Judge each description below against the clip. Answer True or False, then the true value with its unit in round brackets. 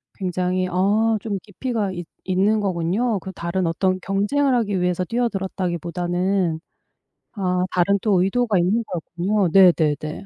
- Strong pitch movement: False (2.6 semitones)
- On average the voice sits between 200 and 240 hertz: False (190 Hz)